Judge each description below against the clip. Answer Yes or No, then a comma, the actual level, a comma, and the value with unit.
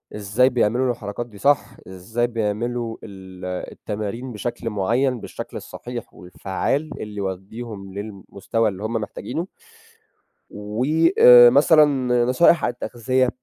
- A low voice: Yes, low, 115 Hz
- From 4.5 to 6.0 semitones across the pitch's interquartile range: No, average, 3.2 semitones